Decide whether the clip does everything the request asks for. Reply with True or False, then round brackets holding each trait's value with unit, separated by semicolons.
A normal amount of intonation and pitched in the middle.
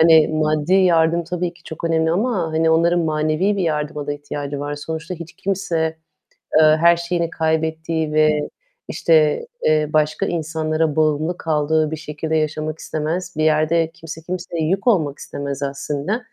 False (1.7 semitones; 160 Hz)